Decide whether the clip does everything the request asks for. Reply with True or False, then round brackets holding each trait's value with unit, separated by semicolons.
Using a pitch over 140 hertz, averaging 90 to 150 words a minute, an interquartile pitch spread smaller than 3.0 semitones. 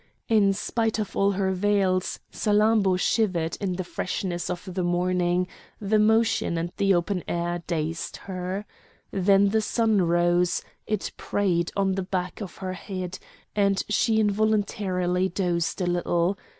True (190 Hz; 145 wpm; 2.6 semitones)